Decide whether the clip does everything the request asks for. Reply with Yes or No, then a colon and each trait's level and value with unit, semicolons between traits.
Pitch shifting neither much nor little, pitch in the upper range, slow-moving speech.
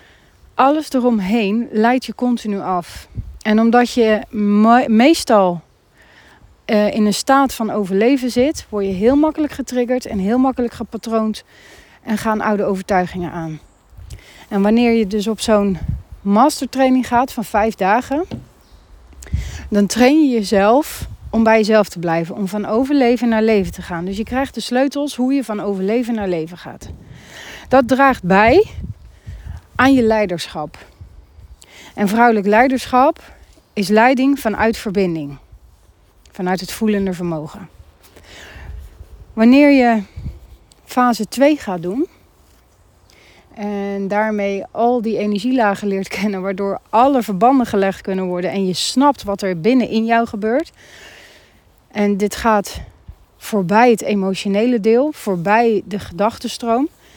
Yes: average, 4.0 semitones; high, 215 Hz; slow, 130 wpm